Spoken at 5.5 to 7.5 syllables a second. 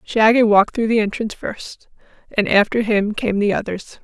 No: 5.1 syllables/s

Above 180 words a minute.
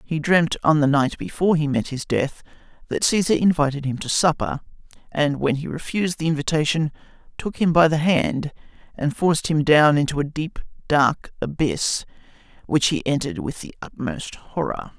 No: average, 170 wpm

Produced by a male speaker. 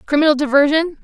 No: female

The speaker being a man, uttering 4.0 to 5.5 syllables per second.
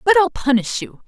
No: female; 5.4 syllables/s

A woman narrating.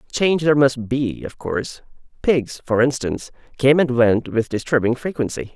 No: male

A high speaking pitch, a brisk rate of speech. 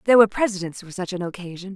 Yes: high, 195 Hz; fast, 240 wpm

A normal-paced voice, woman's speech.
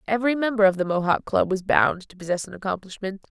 No: fast, 210 wpm; female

